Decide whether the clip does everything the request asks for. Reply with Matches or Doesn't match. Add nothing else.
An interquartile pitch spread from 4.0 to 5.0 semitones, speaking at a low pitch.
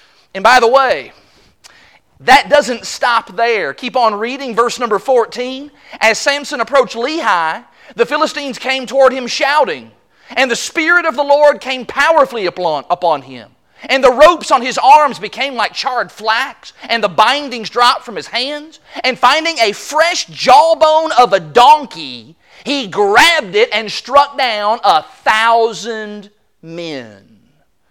Doesn't match